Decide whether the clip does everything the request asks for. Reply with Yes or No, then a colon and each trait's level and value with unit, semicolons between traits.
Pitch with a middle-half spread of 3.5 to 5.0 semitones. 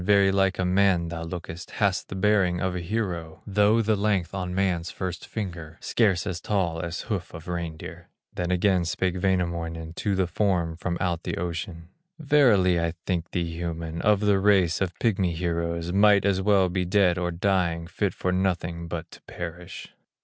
No: narrow, 2.6 semitones